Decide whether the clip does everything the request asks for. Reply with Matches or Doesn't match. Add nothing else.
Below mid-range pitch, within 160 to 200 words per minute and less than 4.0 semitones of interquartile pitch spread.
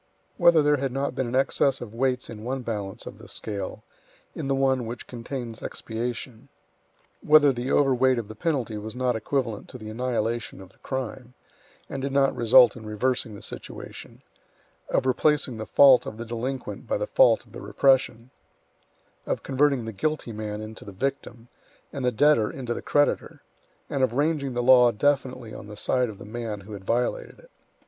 Matches